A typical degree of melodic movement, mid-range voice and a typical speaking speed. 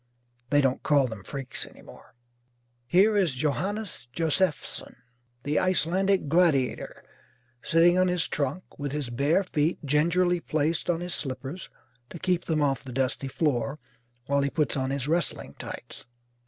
Yes: average, 4.4 semitones; medium, 150 Hz; average, 150 wpm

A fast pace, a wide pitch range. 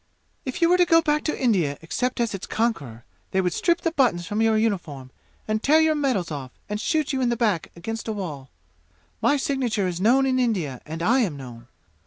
Yes: fast, 220 wpm; wide, 7.7 semitones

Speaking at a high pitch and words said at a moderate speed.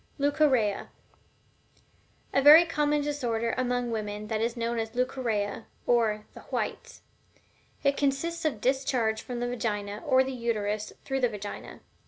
Yes: high, 240 Hz; average, 145 wpm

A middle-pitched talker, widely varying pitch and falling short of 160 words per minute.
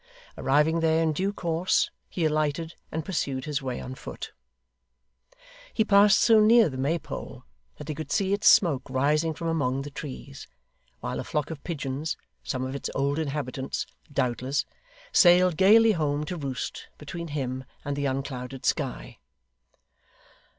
No: medium, 150 Hz; average, 3.7 semitones; average, 150 wpm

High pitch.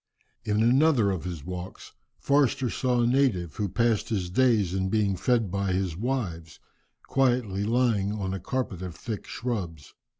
No: low, 105 Hz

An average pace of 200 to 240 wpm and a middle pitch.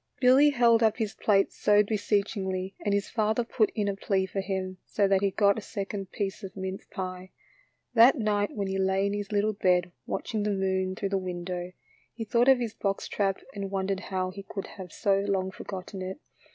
No: fast, 205 wpm; high, 195 Hz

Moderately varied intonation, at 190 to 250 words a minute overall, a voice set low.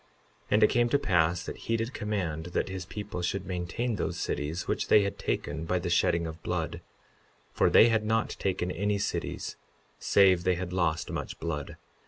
Yes: average, 3.5 semitones; average, 195 wpm; very low, 90 Hz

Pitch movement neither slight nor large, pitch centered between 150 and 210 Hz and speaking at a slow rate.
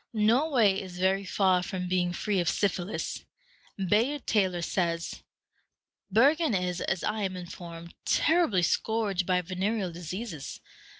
Yes: average, 3.2 semitones; high, 190 Hz; slow, 125 wpm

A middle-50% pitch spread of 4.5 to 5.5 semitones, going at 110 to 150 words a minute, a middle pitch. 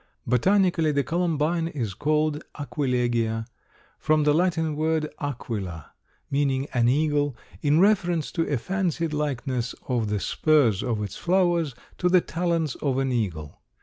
Yes: average, 5.0 semitones; average, 140 wpm; medium, 145 Hz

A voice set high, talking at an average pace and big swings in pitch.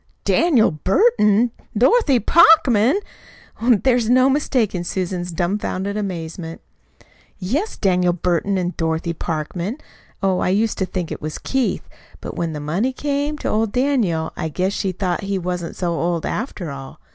Yes: high, 195 Hz; average, 150 wpm; wide, 6.1 semitones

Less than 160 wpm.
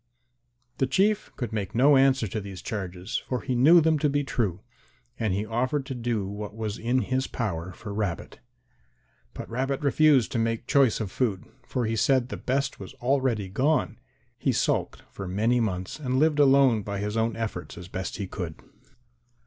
No: average, 185 wpm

